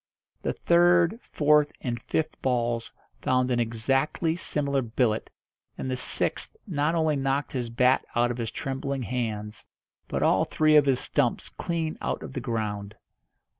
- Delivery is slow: No, average, 155 wpm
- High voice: No, low, 130 Hz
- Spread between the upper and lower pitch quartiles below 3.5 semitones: No, average, 4.2 semitones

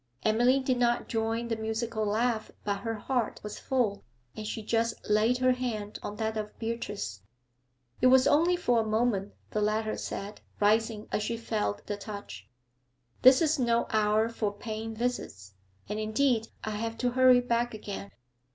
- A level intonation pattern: Yes, narrow, 2.3 semitones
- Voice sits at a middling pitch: No, high, 225 Hz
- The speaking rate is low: No, average, 170 wpm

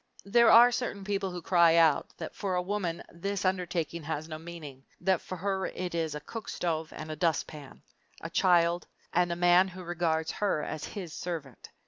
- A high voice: No, medium, 175 Hz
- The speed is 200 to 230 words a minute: No, average, 190 wpm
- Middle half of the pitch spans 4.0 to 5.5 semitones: No, average, 2.9 semitones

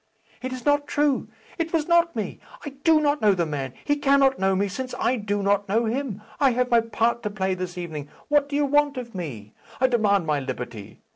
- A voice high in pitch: Yes, high, 230 Hz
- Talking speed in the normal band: No, fast, 225 wpm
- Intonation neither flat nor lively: No, wide, 7.0 semitones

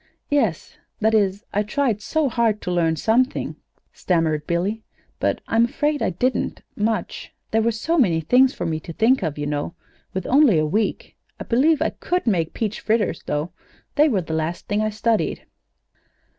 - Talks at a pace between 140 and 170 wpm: No, average, 180 wpm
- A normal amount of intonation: No, wide, 6.0 semitones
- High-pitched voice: Yes, high, 215 Hz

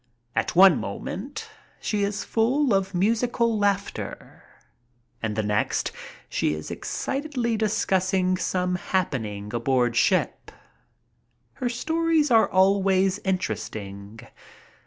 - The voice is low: No, high, 190 Hz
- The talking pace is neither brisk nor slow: No, slow, 100 wpm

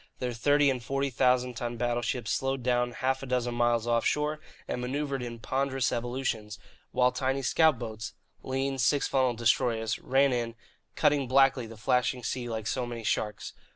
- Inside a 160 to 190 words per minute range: Yes, average, 165 wpm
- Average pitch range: No, narrow, 2.1 semitones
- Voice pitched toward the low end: Yes, low, 125 Hz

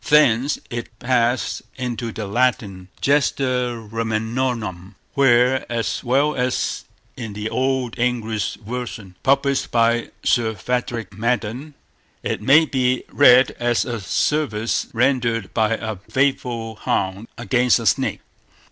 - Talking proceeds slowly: Yes, slow, 120 wpm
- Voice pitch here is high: No, low, 120 Hz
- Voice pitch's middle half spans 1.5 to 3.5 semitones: Yes, narrow, 2.5 semitones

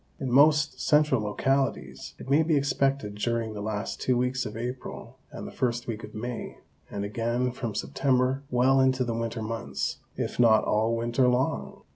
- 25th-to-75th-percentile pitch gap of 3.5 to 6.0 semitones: No, average, 2.7 semitones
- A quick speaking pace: No, average, 175 wpm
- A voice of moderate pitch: No, low, 125 Hz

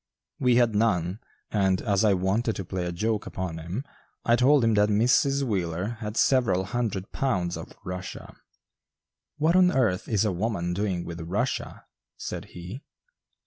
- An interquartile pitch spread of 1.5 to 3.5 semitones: No, average, 4.6 semitones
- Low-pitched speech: Yes, low, 105 Hz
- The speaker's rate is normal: Yes, average, 160 wpm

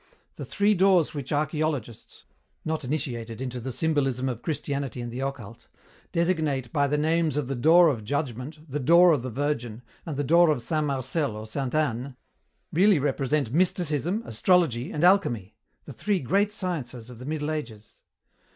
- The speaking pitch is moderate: Yes, medium, 145 Hz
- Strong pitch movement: No, average, 4.4 semitones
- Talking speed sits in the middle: Yes, average, 170 wpm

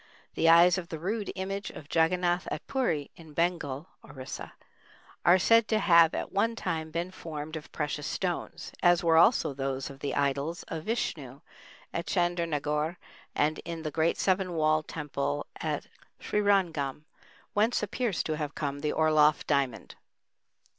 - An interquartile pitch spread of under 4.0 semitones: Yes, average, 3.4 semitones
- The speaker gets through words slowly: No, average, 155 wpm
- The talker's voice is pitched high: No, medium, 165 Hz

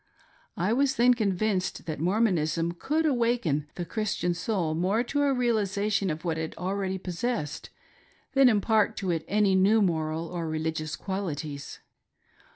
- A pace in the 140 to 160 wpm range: Yes, average, 150 wpm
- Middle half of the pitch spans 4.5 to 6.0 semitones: Yes, average, 5.1 semitones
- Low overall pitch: No, high, 190 Hz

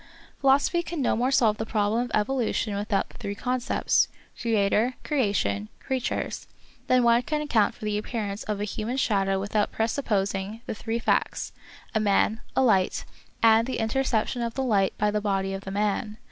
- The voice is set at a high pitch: Yes, high, 220 Hz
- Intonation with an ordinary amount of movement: Yes, average, 3.2 semitones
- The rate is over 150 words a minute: Yes, average, 180 wpm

